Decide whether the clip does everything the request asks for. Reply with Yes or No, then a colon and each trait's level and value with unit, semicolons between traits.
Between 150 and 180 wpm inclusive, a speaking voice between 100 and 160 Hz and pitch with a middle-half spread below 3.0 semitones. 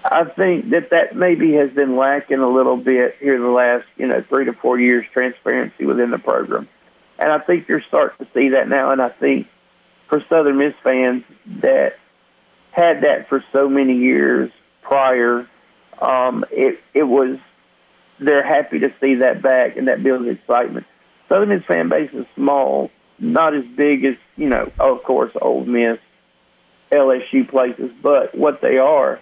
Yes: average, 175 wpm; low, 135 Hz; narrow, 2.5 semitones